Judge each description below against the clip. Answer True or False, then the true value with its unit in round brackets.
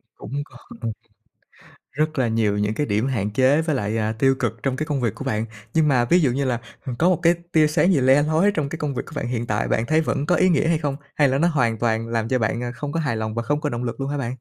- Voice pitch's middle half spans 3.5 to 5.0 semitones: True (4.7 semitones)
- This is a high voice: False (135 Hz)